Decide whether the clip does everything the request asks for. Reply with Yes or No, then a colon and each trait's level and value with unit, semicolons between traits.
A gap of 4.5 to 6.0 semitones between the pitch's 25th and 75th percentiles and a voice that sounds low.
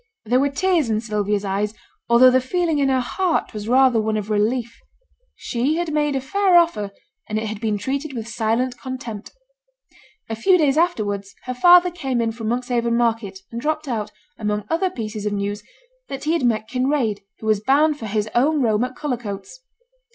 No: average, 5.0 semitones; high, 240 Hz